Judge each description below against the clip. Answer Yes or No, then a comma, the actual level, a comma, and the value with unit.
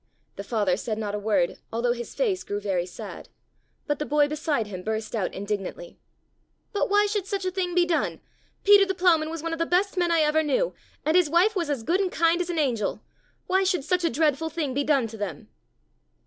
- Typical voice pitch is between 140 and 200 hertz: No, very high, 310 Hz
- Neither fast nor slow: No, fast, 225 wpm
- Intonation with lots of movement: Yes, wide, 8.3 semitones